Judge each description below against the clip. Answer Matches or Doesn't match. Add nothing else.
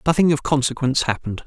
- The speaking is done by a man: Matches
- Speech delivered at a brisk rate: Doesn't match